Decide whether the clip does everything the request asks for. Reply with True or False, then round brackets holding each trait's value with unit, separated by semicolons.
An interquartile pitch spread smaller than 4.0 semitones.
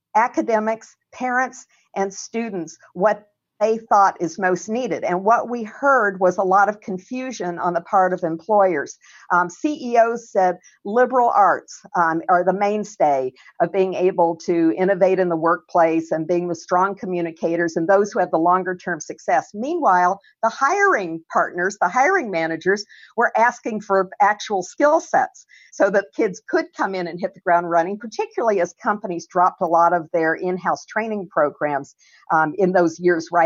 False (4.3 semitones)